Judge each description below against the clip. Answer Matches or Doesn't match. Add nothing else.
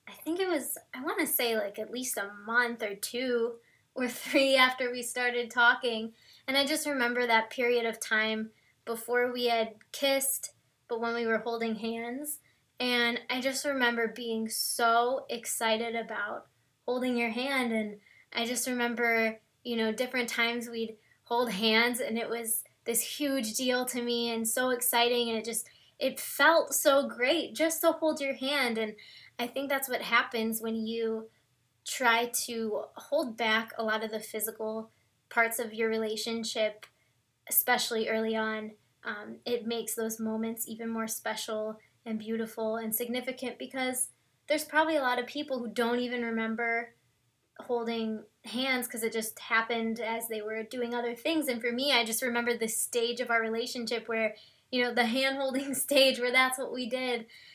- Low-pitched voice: Doesn't match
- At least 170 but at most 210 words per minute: Matches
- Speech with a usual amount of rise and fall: Doesn't match